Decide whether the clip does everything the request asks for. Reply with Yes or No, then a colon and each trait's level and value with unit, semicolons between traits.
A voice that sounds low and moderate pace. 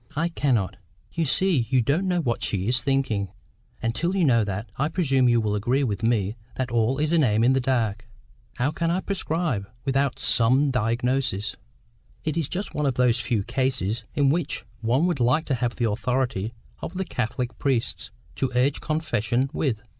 Yes: low, 125 Hz; average, 190 wpm